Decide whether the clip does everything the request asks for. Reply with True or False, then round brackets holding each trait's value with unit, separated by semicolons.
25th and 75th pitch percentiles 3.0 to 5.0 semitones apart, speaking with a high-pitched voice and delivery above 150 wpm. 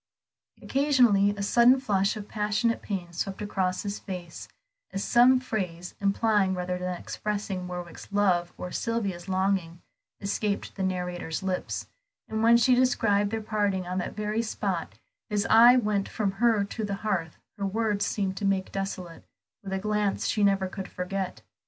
False (2.4 semitones; 200 Hz; 160 wpm)